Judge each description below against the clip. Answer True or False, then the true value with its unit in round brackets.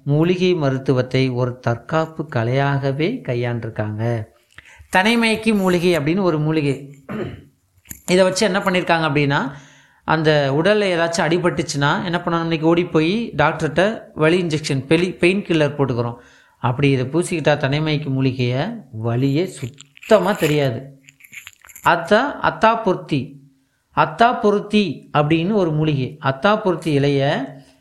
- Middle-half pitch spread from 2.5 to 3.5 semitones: False (4.6 semitones)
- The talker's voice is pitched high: False (155 Hz)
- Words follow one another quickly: False (110 wpm)